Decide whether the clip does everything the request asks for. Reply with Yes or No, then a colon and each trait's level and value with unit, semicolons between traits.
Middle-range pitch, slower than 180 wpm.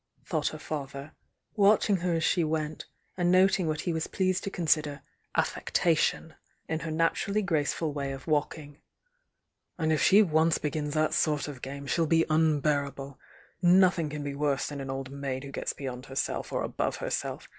No: medium, 155 Hz; average, 185 wpm